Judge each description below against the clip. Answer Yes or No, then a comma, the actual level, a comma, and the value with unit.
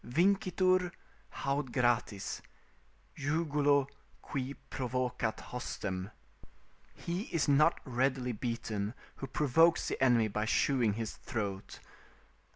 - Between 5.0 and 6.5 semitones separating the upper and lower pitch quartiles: No, average, 4.2 semitones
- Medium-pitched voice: No, low, 130 Hz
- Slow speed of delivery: Yes, slow, 100 wpm